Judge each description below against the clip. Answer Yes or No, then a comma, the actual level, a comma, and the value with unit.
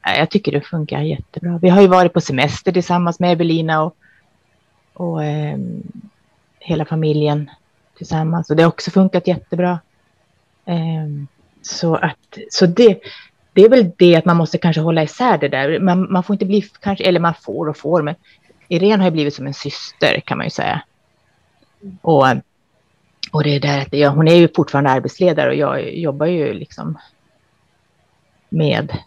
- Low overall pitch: No, medium, 170 Hz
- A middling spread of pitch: Yes, average, 3.3 semitones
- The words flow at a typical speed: Yes, average, 175 wpm